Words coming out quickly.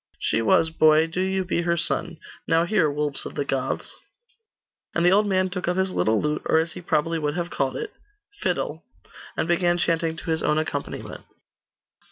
No: average, 195 wpm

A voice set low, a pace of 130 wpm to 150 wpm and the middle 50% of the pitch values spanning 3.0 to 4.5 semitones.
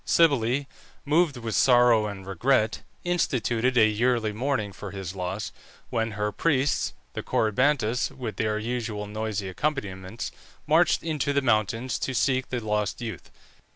Yes: low, 115 Hz; average, 140 wpm; average, 3.8 semitones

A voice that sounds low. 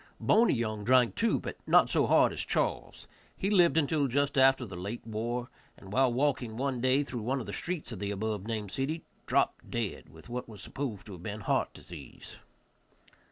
Yes: low, 120 Hz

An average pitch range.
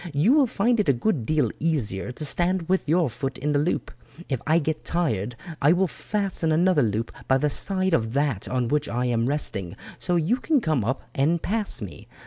No: wide, 6.2 semitones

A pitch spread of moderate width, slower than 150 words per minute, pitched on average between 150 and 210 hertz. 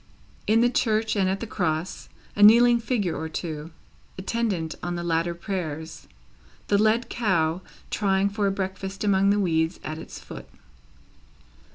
No: average, 4.4 semitones; average, 155 wpm; high, 190 Hz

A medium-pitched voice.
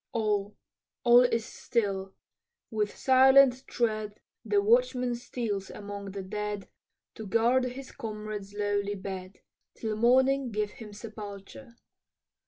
No: high, 215 Hz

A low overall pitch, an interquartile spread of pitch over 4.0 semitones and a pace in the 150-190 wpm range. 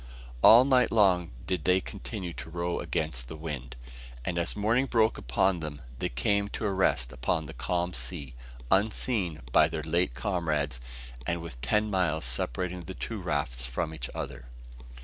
Yes: very low, 85 Hz; average, 5.0 semitones; average, 170 wpm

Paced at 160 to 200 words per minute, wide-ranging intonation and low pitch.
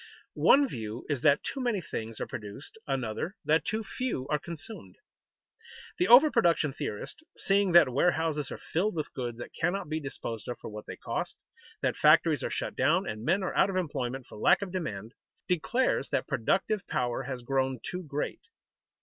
No: average, 185 wpm; wide, 7.4 semitones; medium, 150 Hz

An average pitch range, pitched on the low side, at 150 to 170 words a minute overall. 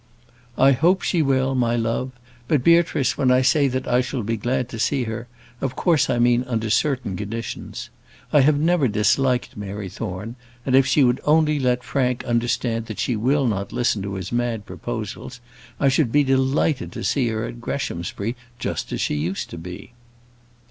No: average, 3.3 semitones; low, 125 Hz; average, 185 wpm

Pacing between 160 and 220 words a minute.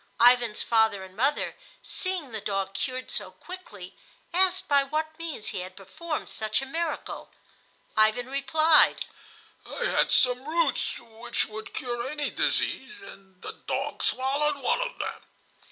No: average, 145 wpm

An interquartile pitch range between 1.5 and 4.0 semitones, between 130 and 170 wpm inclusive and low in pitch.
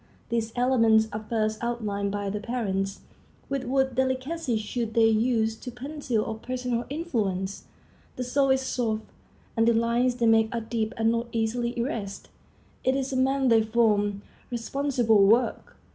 No: narrow, 2.6 semitones; average, 160 wpm; high, 235 Hz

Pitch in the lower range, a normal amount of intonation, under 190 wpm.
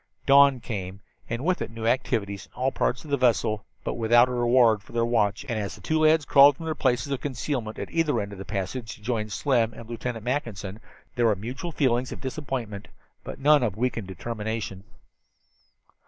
No: low, 120 Hz; average, 3.7 semitones; average, 200 wpm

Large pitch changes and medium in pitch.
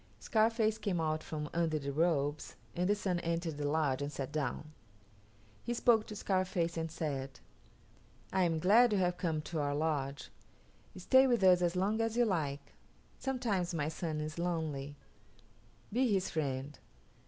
No: average, 4.7 semitones; medium, 170 Hz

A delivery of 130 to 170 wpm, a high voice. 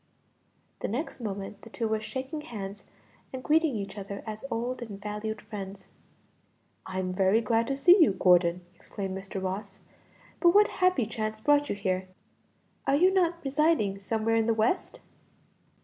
Yes: average, 160 wpm; high, 220 Hz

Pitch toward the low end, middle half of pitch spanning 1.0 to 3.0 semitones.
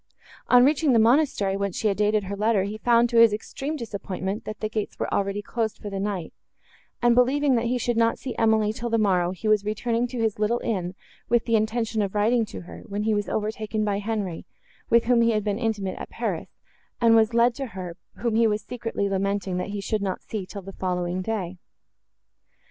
No: high, 215 Hz; narrow, 2.6 semitones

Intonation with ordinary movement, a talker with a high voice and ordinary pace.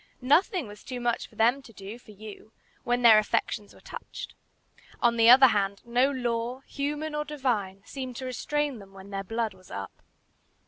Yes: average, 4.1 semitones; high, 235 Hz; average, 185 wpm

